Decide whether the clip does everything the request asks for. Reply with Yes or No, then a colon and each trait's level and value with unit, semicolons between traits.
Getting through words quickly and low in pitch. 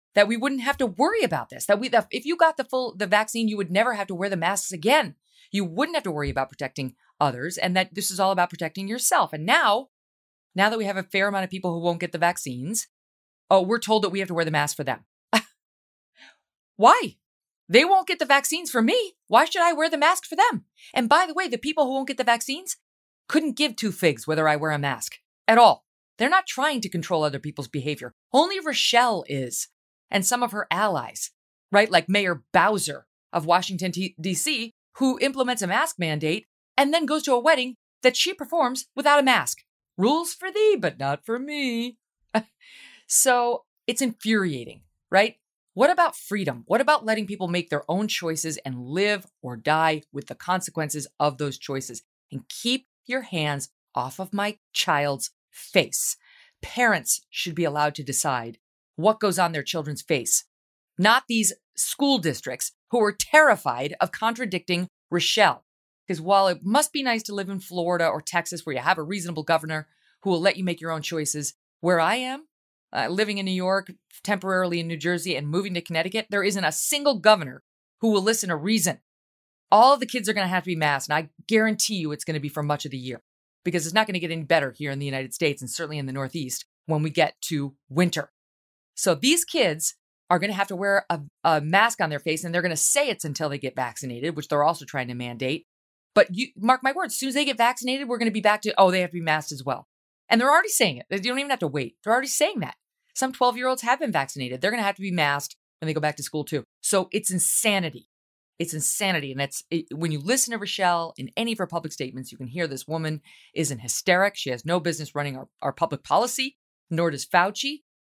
No: fast, 225 wpm; medium, 185 Hz